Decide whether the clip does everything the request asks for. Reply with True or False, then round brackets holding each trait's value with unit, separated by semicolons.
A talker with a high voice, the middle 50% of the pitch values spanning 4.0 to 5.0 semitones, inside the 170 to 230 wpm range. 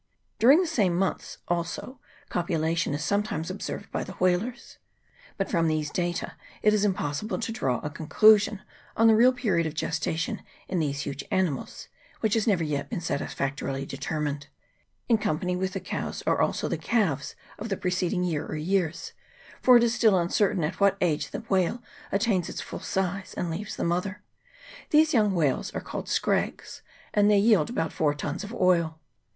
False (180 Hz; 4.7 semitones; 180 wpm)